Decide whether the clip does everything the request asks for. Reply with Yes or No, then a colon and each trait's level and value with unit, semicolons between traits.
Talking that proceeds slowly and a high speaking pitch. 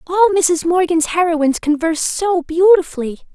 Yes: slow, 125 wpm; very high, 340 Hz